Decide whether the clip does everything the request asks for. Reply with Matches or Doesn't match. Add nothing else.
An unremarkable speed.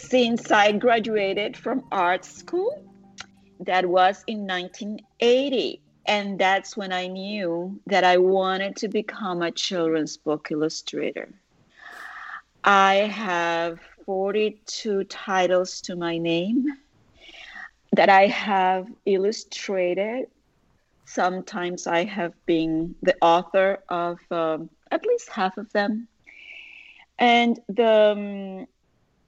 Doesn't match